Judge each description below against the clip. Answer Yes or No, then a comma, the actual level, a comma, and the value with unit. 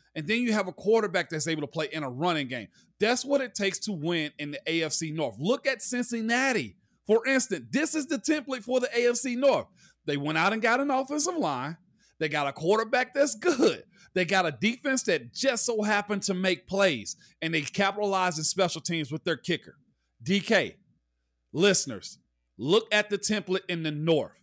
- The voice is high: Yes, high, 195 Hz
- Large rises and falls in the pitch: Yes, wide, 7.0 semitones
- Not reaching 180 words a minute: No, average, 195 wpm